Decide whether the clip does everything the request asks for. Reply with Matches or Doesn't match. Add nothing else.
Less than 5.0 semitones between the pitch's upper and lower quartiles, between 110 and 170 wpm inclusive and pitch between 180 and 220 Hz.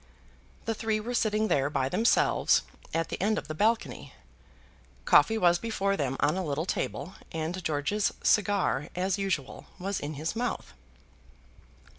Doesn't match